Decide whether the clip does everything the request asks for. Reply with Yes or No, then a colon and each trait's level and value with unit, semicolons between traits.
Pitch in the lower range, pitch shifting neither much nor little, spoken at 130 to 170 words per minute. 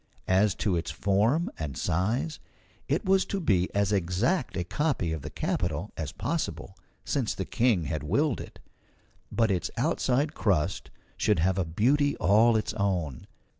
No: low, 100 Hz; wide, 6.4 semitones; average, 160 wpm